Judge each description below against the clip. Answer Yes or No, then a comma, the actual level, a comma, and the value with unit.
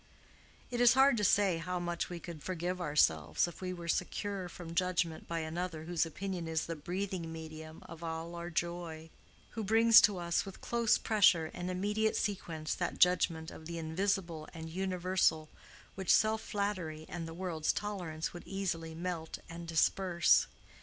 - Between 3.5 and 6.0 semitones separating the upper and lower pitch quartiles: No, average, 2.8 semitones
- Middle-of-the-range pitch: Yes, medium, 175 Hz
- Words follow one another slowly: No, average, 165 wpm